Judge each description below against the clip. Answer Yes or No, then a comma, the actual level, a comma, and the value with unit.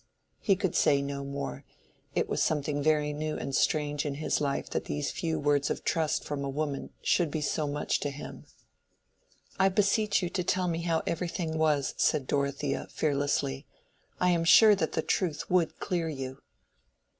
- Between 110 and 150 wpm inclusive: No, average, 180 wpm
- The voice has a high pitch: No, medium, 150 Hz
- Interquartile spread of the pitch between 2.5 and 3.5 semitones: Yes, average, 3.1 semitones